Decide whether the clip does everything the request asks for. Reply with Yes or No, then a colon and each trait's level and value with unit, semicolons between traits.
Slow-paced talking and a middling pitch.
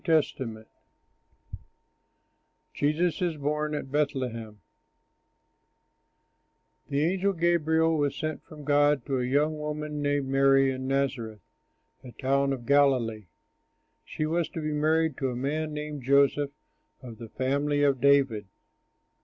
Yes: slow, 130 wpm; medium, 145 Hz